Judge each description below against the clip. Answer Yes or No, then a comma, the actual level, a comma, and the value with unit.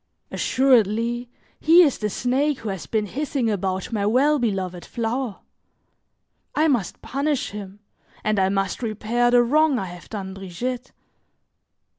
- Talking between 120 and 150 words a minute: Yes, average, 140 wpm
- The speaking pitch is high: Yes, high, 230 Hz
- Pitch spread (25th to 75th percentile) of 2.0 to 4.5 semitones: No, average, 4.9 semitones